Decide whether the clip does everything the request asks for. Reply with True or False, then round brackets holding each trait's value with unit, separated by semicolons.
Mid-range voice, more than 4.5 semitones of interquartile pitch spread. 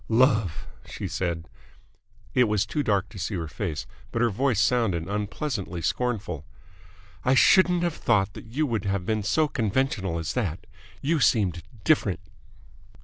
False (105 Hz; 4.9 semitones)